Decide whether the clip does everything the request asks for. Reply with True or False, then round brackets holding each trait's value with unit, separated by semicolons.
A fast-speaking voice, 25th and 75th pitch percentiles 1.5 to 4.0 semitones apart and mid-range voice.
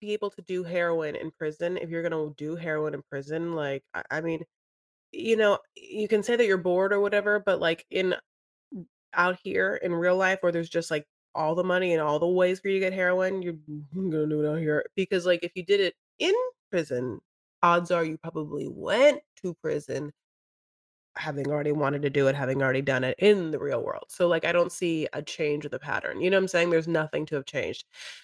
True (225 wpm; 3.7 semitones; 170 Hz)